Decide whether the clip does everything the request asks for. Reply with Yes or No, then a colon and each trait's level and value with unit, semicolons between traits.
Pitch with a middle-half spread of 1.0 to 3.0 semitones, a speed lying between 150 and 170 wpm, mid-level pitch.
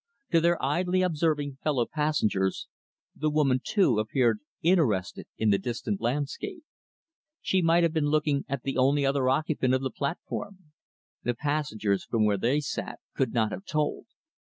No: average, 4.5 semitones; average, 155 wpm; medium, 145 Hz